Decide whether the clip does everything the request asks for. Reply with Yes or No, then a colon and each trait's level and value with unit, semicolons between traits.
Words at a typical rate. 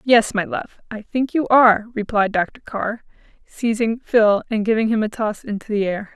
Yes: average, 195 wpm